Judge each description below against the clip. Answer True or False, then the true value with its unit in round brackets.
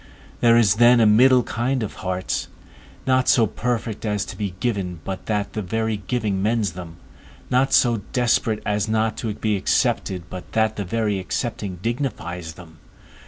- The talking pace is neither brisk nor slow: True (165 wpm)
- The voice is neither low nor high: False (110 Hz)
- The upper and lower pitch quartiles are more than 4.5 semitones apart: False (3.5 semitones)